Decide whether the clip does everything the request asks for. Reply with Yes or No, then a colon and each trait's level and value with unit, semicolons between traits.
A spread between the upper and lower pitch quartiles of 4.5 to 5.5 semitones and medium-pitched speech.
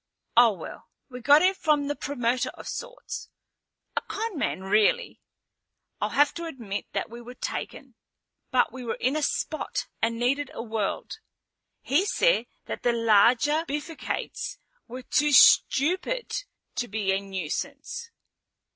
No: average, 5.2 semitones; very high, 260 Hz